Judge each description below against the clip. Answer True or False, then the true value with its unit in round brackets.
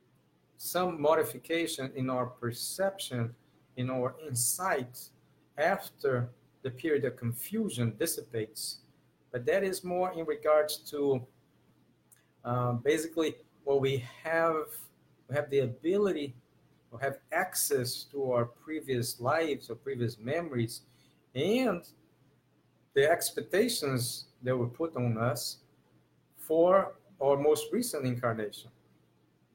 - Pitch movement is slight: False (4.6 semitones)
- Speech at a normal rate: False (110 wpm)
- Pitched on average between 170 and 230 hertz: False (135 Hz)